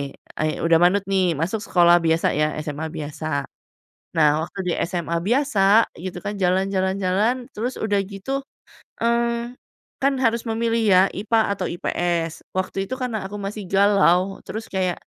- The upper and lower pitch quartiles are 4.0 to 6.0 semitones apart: Yes, average, 4.4 semitones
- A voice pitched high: Yes, high, 195 Hz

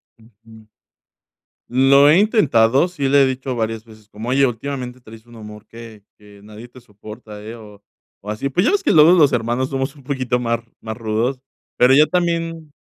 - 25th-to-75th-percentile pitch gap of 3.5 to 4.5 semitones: Yes, average, 3.9 semitones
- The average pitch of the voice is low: Yes, low, 125 Hz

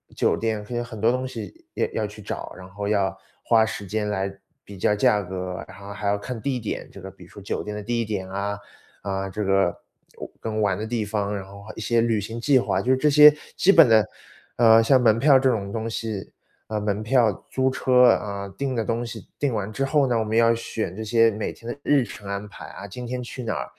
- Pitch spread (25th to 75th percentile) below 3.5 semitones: Yes, average, 3.0 semitones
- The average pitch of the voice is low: Yes, low, 110 Hz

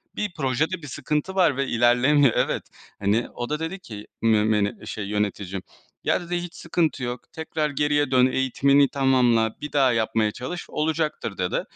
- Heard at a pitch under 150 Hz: Yes, low, 135 Hz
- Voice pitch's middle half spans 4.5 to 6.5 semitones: Yes, average, 5.1 semitones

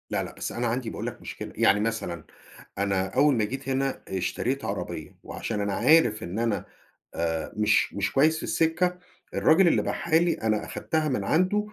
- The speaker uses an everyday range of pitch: No, wide, 7.5 semitones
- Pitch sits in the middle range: No, low, 120 Hz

